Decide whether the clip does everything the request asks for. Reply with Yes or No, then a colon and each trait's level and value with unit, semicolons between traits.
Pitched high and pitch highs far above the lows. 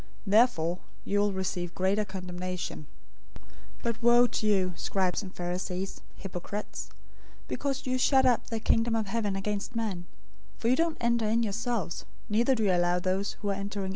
No: high, 205 Hz; average, 3.9 semitones